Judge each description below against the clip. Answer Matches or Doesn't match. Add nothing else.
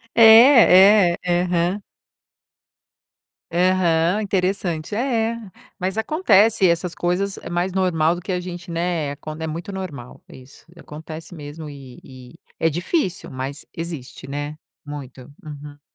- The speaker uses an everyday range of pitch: Matches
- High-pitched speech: Doesn't match